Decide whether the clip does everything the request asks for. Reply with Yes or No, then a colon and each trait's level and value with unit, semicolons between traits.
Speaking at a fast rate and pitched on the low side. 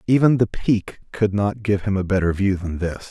Yes: fast, 230 wpm; low, 100 Hz